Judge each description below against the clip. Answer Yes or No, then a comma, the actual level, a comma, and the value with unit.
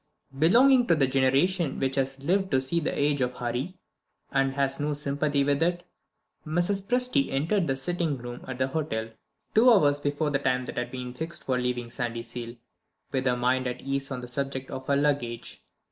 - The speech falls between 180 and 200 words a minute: Yes, average, 190 wpm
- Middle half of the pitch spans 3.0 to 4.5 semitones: Yes, average, 3.8 semitones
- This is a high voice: No, low, 135 Hz